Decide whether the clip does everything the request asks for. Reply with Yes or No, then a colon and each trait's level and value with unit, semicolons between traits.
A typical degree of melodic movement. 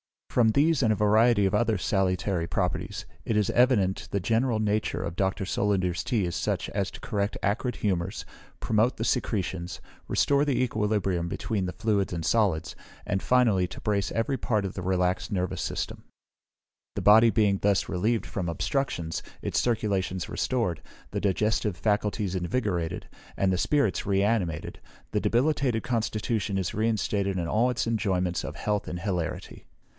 Yes: average, 3.3 semitones